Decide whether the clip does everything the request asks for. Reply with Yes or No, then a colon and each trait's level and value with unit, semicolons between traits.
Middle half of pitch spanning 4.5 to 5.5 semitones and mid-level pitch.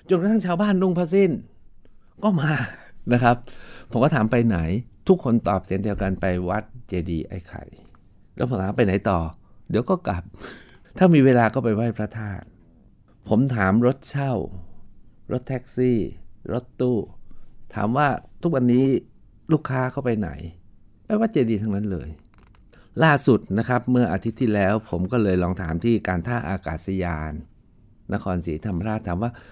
No: average, 4.8 semitones; low, 110 Hz